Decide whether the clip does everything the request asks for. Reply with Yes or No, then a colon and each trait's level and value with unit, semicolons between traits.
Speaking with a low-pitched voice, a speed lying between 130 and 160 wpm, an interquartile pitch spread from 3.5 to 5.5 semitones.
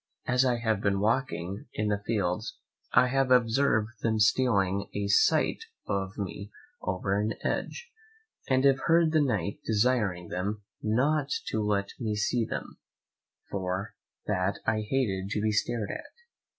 Yes: low, 105 Hz; average, 150 wpm; average, 3.9 semitones